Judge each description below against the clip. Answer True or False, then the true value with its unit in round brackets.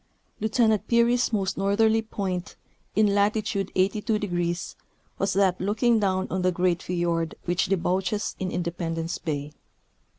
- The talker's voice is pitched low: False (190 Hz)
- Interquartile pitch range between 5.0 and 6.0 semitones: False (3.1 semitones)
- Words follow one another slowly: True (130 wpm)